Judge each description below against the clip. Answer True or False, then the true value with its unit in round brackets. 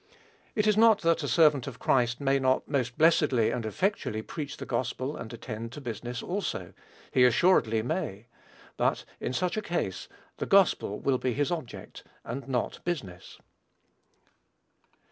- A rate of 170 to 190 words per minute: False (155 wpm)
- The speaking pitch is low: True (130 Hz)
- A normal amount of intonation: False (6.0 semitones)